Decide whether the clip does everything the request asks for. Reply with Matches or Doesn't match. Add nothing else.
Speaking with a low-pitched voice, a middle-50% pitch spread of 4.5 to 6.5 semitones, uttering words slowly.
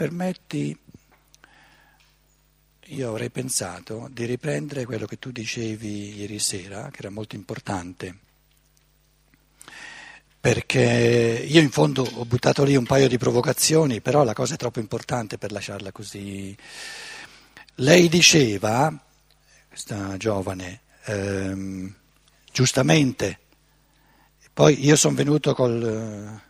Matches